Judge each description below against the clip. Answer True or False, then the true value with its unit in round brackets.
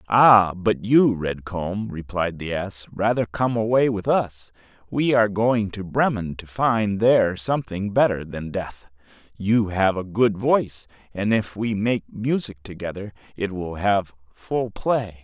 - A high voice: False (105 Hz)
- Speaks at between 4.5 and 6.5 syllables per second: False (4.0 syllables/s)